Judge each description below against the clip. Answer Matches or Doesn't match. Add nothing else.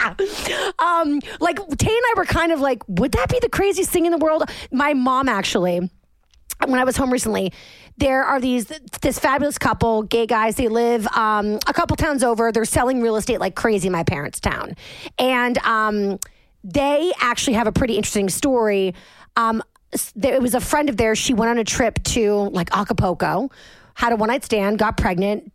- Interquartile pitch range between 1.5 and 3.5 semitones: Doesn't match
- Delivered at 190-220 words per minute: Matches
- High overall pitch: Matches